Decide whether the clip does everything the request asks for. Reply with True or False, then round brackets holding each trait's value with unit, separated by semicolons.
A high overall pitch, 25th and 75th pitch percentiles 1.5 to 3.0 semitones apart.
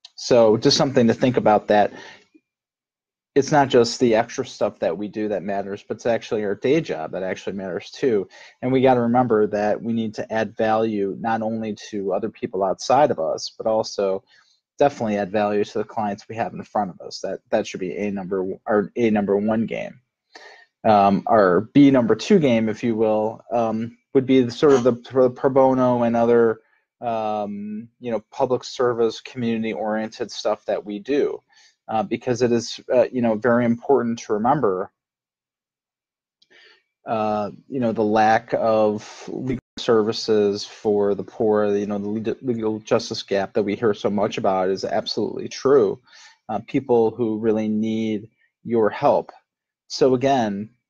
False (110 Hz; 2.7 semitones)